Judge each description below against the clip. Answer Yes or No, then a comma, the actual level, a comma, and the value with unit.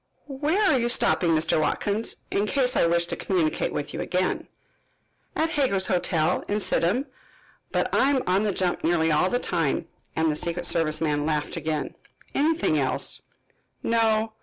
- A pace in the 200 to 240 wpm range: No, average, 165 wpm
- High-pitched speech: No, medium, 180 Hz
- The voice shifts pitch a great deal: Yes, wide, 6.3 semitones